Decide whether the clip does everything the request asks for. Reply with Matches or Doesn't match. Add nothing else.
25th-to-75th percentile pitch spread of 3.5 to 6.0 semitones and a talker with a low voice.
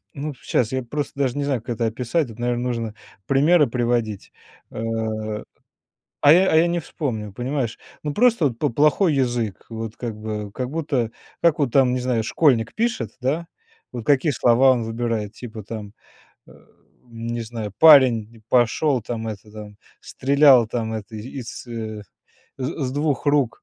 Matches